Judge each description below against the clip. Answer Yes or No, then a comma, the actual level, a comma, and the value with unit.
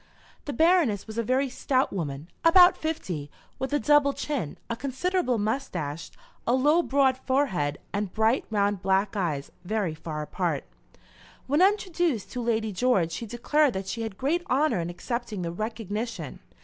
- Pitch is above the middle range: Yes, high, 230 Hz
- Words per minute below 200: Yes, average, 165 wpm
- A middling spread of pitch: No, wide, 6.7 semitones